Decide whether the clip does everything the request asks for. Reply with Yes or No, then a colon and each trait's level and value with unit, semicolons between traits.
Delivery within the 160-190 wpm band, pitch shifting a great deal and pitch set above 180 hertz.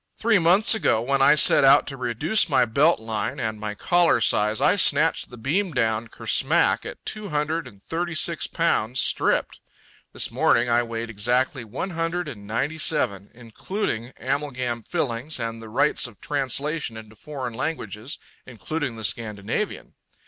No: average, 165 wpm; wide, 5.9 semitones; low, 130 Hz